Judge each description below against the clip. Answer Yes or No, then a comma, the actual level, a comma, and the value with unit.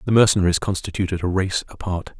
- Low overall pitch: Yes, very low, 95 Hz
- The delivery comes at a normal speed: Yes, average, 165 wpm